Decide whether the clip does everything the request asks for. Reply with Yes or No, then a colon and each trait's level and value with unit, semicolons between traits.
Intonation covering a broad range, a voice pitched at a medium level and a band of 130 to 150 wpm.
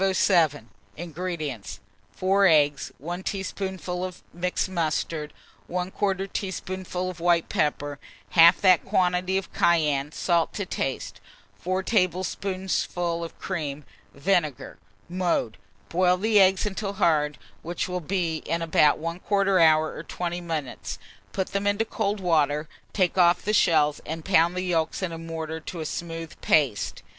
No: average, 2.9 semitones; medium, 175 Hz; average, 140 wpm